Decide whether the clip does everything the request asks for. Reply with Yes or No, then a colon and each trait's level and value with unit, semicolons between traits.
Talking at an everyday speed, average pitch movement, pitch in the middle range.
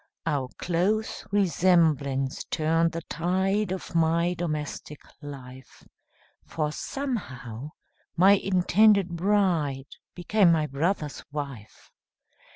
No: slow, 90 wpm; average, 4.5 semitones; medium, 165 Hz